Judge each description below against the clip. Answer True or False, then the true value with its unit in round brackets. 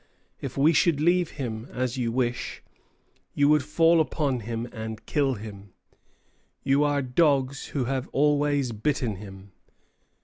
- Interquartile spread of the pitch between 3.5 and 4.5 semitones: True (4.1 semitones)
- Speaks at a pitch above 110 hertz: True (135 Hz)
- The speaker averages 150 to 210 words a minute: False (140 wpm)